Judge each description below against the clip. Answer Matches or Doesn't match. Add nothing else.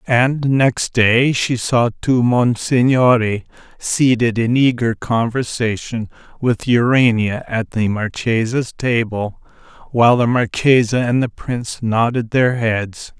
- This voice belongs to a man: Matches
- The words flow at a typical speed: Doesn't match